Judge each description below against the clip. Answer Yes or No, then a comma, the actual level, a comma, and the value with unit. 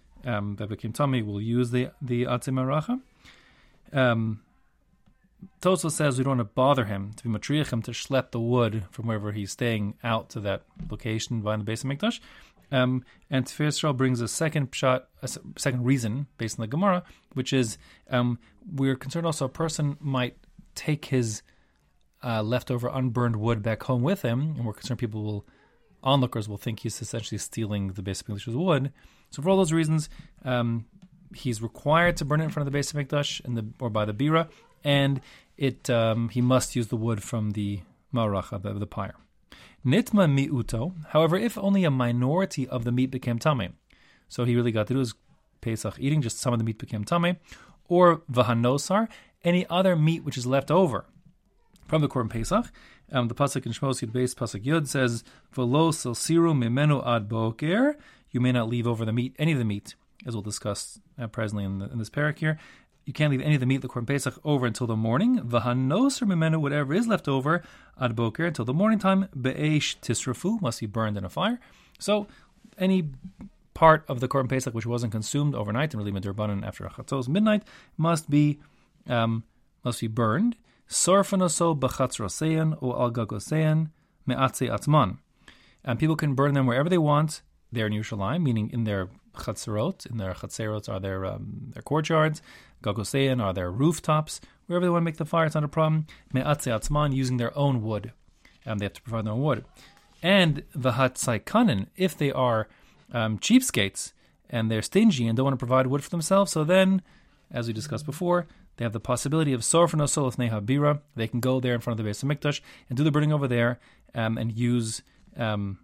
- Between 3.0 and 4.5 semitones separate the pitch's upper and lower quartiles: No, average, 5.3 semitones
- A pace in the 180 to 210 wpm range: Yes, average, 190 wpm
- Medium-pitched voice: No, low, 130 Hz